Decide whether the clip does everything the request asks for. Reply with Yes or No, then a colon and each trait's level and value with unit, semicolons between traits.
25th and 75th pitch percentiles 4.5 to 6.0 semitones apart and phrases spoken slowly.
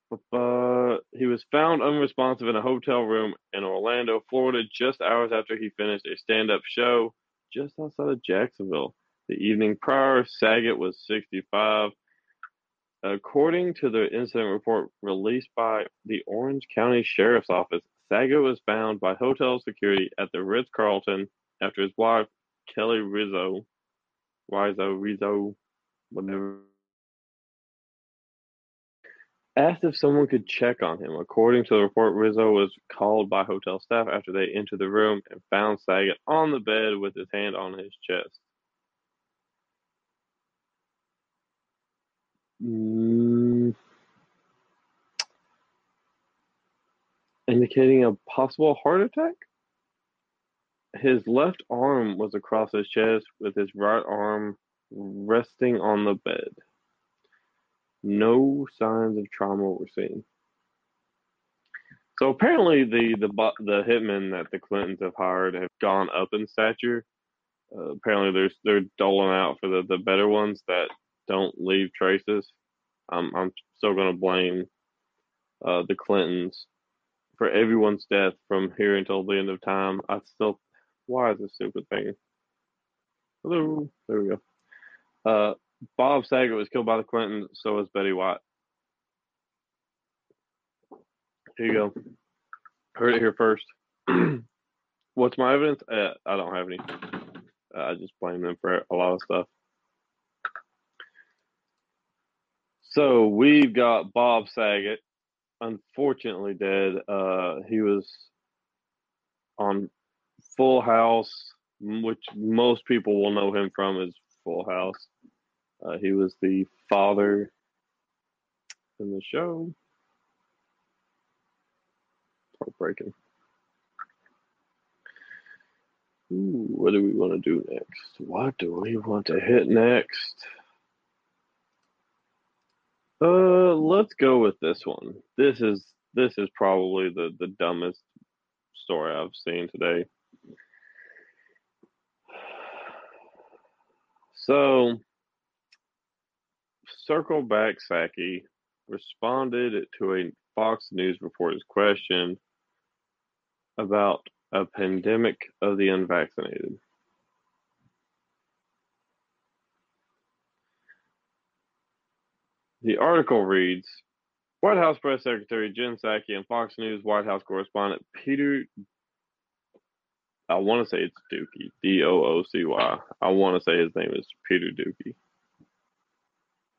No: average, 3.7 semitones; slow, 115 wpm